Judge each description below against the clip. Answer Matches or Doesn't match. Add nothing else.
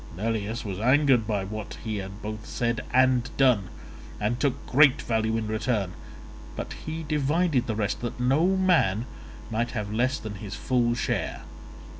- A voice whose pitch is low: Matches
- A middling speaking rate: Matches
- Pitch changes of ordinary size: Matches